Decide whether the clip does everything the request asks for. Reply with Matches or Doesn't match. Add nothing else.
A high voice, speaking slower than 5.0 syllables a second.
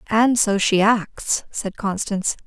Matches